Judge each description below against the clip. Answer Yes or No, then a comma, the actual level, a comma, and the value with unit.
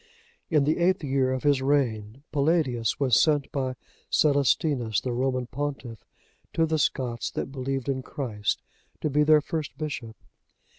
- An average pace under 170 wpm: Yes, average, 150 wpm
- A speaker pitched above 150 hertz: No, low, 135 Hz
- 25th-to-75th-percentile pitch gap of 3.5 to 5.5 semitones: No, average, 2.9 semitones